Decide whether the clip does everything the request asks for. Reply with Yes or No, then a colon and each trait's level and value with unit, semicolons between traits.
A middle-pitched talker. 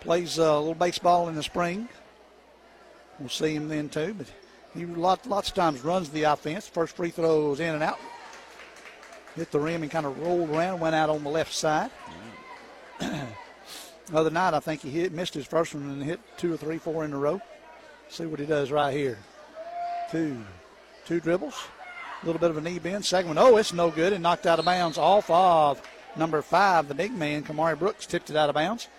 Yes: medium, 165 Hz